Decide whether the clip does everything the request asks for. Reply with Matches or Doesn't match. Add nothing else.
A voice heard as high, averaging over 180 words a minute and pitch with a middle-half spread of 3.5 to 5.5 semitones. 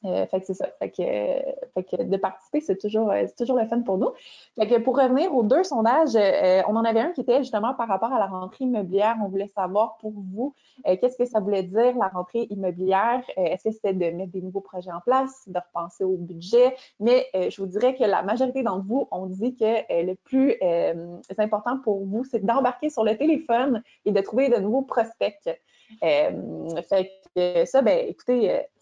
Matches